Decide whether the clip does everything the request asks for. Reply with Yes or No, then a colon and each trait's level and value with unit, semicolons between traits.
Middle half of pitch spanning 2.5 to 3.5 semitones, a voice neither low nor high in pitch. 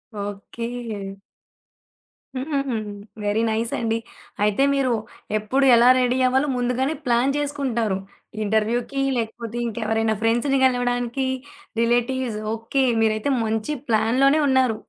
No: average, 2.9 semitones; high, 240 Hz